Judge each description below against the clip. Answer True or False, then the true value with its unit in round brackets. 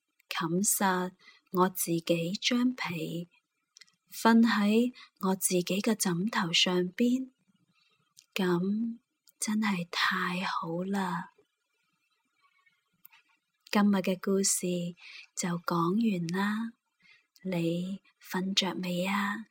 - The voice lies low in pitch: False (190 Hz)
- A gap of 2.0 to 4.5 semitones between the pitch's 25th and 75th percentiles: True (3.3 semitones)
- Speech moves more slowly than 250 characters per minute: True (115 characters per minute)